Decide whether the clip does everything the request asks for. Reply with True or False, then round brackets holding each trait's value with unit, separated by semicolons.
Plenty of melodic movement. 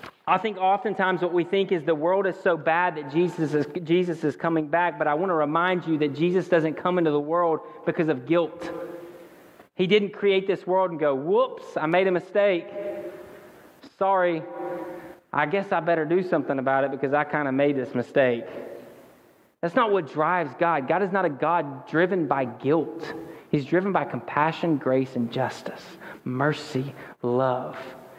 False (3.7 semitones)